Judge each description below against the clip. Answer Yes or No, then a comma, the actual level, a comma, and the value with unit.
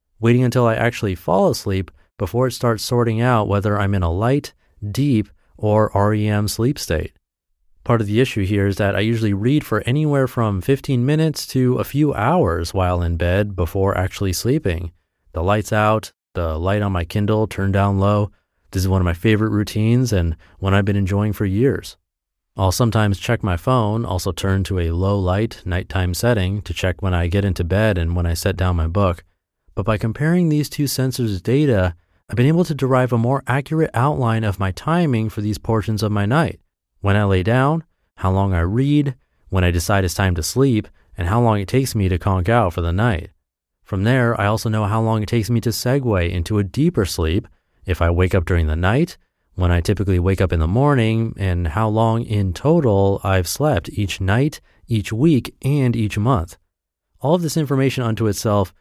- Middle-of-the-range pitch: No, low, 105 Hz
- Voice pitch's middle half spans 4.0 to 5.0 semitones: Yes, average, 4.5 semitones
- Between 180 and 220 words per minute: Yes, fast, 205 wpm